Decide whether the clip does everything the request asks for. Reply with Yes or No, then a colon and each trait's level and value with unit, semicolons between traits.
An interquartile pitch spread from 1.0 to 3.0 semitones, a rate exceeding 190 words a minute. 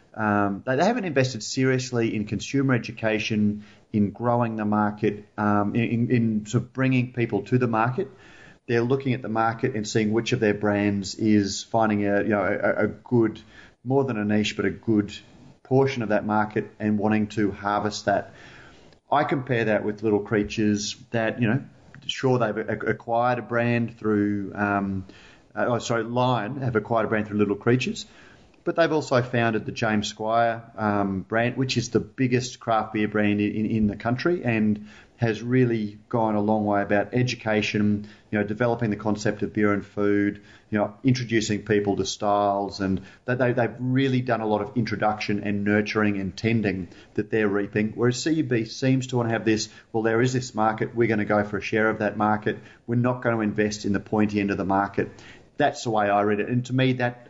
Yes: narrow, 2.4 semitones; average, 200 wpm